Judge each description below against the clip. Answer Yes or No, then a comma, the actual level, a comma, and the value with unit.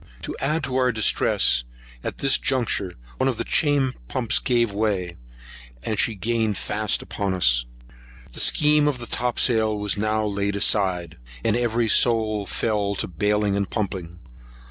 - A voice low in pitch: Yes, low, 110 Hz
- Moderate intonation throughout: Yes, average, 3.2 semitones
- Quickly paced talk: No, average, 155 wpm